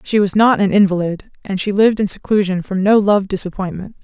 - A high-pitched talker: Yes, high, 195 Hz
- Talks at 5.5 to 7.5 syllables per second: Yes, 5.8 syllables/s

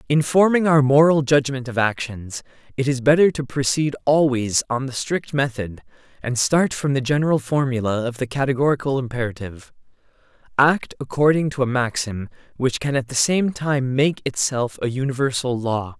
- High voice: No, low, 135 Hz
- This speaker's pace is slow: No, average, 160 wpm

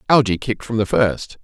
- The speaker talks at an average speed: No, fast, 210 wpm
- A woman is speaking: No, male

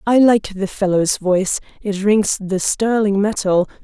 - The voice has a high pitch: Yes, high, 200 Hz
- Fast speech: No, average, 155 wpm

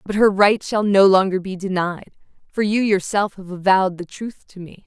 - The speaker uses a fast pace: Yes, fast, 210 wpm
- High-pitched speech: Yes, high, 195 Hz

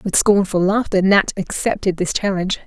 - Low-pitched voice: No, high, 190 Hz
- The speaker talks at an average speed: Yes, average, 155 wpm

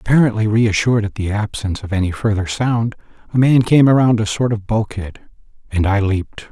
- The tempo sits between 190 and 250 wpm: No, average, 175 wpm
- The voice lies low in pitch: Yes, low, 110 Hz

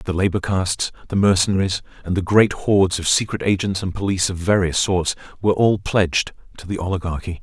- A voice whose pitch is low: Yes, very low, 95 Hz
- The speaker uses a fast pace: No, average, 185 wpm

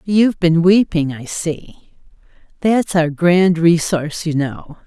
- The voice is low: No, medium, 170 Hz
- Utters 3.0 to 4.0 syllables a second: Yes, 3.8 syllables/s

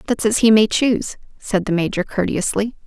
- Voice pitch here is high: Yes, high, 210 Hz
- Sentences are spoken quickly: No, average, 190 wpm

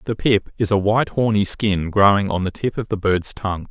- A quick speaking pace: Yes, fast, 245 wpm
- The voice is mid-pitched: No, low, 100 Hz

